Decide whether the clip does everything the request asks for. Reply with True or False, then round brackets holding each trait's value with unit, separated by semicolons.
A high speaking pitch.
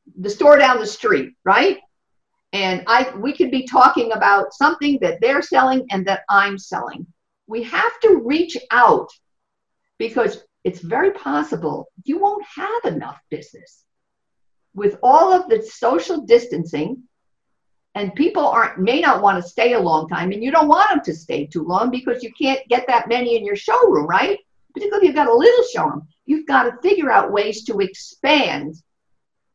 True (260 Hz)